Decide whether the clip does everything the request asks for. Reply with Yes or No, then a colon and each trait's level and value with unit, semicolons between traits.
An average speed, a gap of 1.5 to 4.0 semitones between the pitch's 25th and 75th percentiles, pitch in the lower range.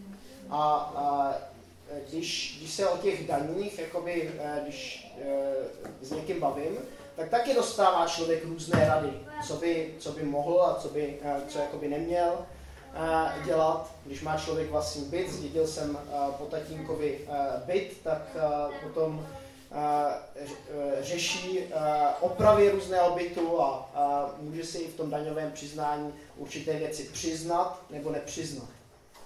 No: average, 140 wpm; narrow, 2.5 semitones; medium, 155 Hz